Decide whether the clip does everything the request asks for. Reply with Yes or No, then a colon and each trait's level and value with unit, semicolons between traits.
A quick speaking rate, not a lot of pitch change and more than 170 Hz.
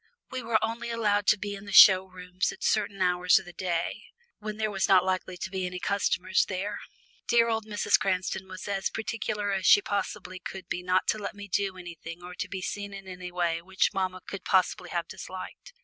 Yes: fast, 210 wpm; narrow, 2.1 semitones; high, 190 Hz